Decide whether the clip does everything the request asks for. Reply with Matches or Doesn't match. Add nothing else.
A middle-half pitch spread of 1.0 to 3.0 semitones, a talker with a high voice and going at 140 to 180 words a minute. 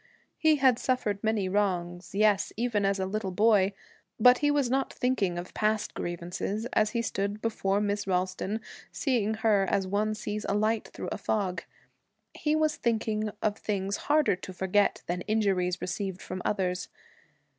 Matches